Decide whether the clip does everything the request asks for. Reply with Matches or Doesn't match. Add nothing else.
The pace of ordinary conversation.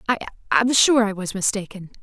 Matches